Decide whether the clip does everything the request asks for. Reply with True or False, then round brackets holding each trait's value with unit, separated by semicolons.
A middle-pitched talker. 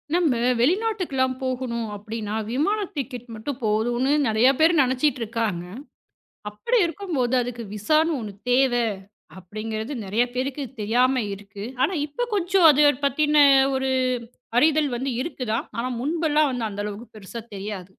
False (255 Hz)